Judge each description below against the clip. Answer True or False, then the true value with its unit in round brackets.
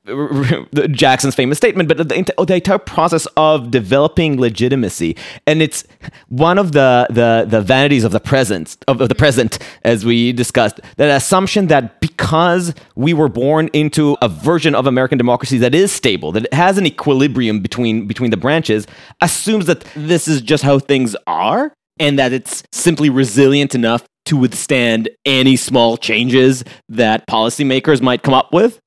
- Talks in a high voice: False (135 Hz)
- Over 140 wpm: True (160 wpm)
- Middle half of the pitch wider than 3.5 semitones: True (4.1 semitones)